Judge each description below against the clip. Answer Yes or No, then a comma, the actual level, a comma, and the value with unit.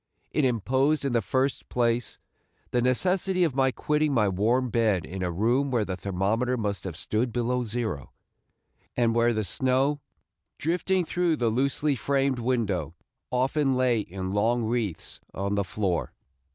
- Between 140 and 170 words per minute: Yes, average, 155 wpm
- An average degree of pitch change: Yes, average, 4.4 semitones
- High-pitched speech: No, low, 120 Hz